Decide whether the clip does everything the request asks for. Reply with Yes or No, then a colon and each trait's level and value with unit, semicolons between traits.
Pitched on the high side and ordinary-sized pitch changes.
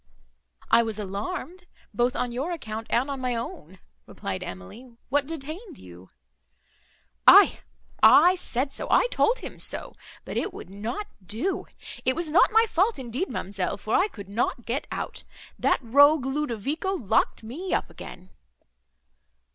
No: very high, 255 Hz; wide, 7.1 semitones